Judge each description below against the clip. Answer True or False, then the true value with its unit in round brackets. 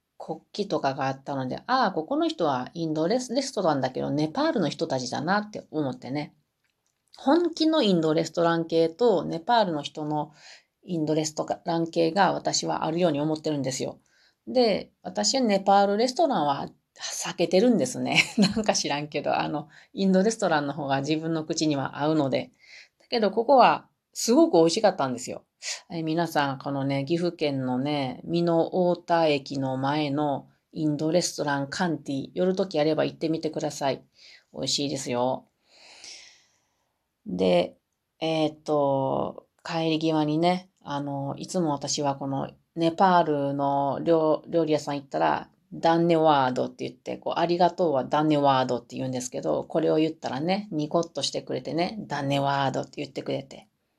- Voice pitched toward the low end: False (155 Hz)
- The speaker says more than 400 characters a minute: False (350 characters per minute)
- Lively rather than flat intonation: False (3.5 semitones)